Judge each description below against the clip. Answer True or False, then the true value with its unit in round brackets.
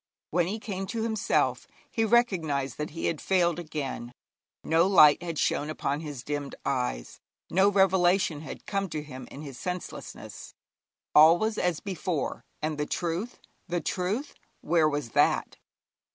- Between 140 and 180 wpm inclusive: True (150 wpm)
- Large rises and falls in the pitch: False (4.5 semitones)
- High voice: False (170 Hz)